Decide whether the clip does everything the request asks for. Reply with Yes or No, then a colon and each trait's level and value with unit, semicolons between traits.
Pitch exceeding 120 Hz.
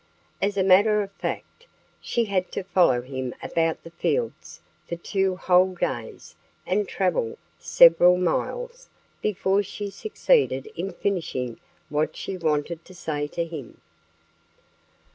Yes: medium, 185 Hz